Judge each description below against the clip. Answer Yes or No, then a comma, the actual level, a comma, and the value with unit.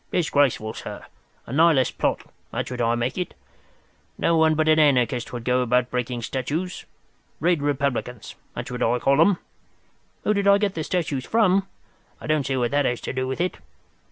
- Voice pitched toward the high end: No, medium, 140 Hz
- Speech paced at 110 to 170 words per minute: No, average, 180 wpm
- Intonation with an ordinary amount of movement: Yes, average, 4.9 semitones